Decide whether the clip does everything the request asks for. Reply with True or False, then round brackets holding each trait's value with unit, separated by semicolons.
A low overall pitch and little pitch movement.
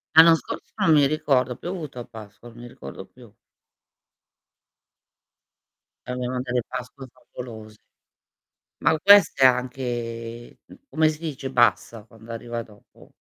False (125 Hz; 3.1 semitones)